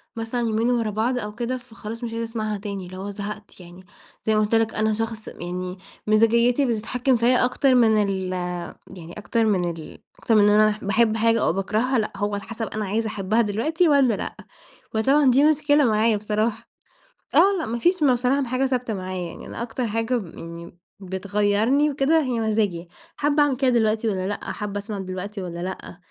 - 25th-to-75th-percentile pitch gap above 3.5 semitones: No, average, 3.2 semitones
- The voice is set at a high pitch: Yes, high, 220 Hz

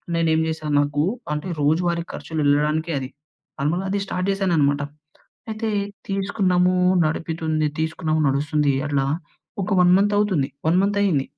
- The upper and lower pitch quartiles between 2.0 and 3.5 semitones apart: No, average, 4.0 semitones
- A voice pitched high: No, medium, 160 Hz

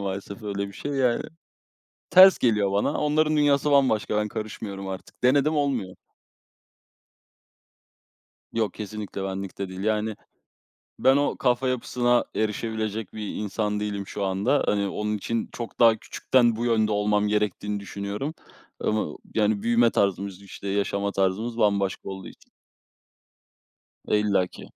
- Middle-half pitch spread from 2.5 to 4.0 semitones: Yes, average, 3.0 semitones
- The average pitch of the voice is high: No, low, 105 Hz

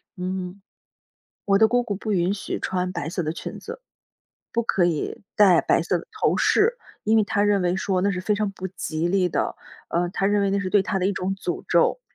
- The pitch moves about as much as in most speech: No, narrow, 2.3 semitones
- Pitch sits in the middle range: No, high, 195 Hz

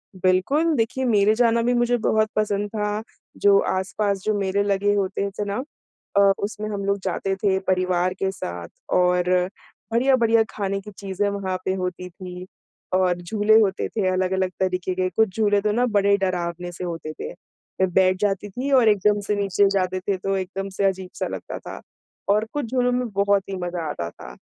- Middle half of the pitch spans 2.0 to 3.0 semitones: Yes, narrow, 2.4 semitones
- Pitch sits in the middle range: No, high, 200 Hz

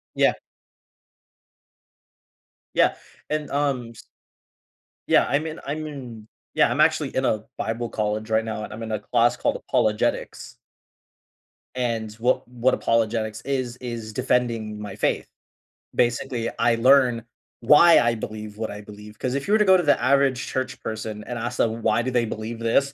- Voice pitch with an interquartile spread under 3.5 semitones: Yes, average, 3.0 semitones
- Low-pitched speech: Yes, low, 115 Hz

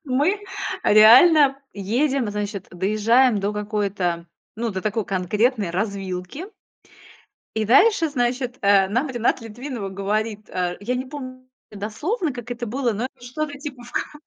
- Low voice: No, high, 230 Hz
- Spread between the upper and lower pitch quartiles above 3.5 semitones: Yes, average, 4.3 semitones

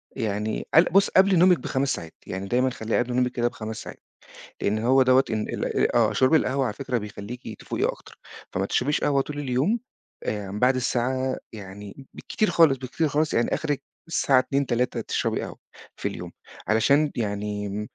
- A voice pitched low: Yes, low, 125 Hz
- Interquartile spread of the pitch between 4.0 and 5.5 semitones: Yes, average, 4.4 semitones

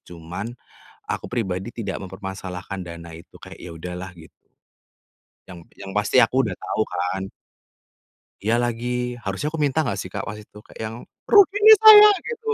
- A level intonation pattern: No, average, 5.3 semitones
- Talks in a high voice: No, low, 105 Hz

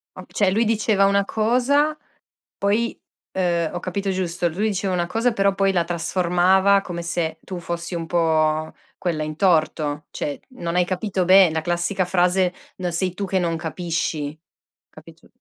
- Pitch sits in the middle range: Yes, medium, 180 Hz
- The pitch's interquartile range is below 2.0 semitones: No, narrow, 2.6 semitones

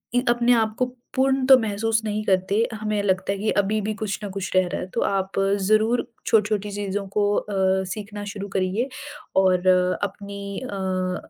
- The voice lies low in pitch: No, high, 205 Hz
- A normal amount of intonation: No, narrow, 1.9 semitones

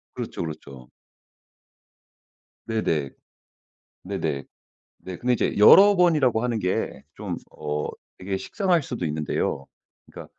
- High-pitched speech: No, very low, 95 Hz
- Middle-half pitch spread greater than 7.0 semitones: Yes, wide, 8.7 semitones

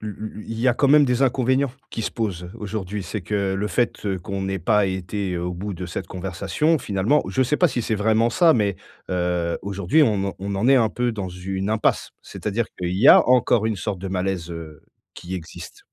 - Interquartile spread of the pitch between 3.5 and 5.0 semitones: Yes, average, 3.9 semitones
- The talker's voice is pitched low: Yes, low, 100 Hz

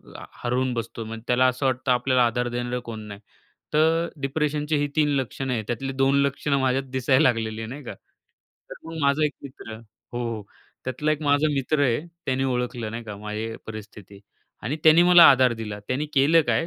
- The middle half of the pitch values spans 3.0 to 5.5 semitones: Yes, average, 3.6 semitones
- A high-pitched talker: No, low, 130 Hz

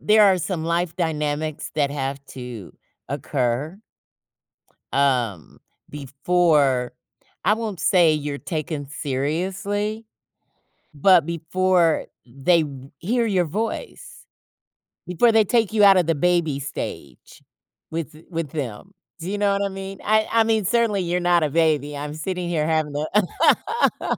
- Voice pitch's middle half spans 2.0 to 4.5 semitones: No, average, 4.9 semitones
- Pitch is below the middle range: No, medium, 165 Hz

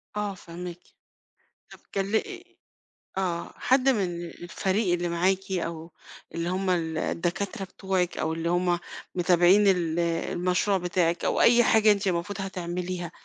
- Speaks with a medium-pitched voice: Yes, medium, 180 Hz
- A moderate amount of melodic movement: No, narrow, 2.1 semitones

